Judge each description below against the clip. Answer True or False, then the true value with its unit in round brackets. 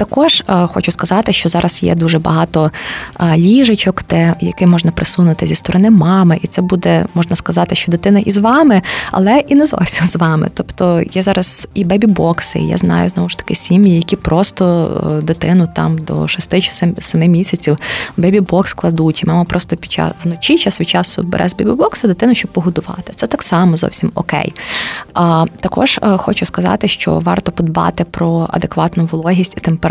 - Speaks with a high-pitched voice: False (175 Hz)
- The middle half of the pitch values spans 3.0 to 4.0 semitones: False (2.5 semitones)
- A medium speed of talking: False (175 wpm)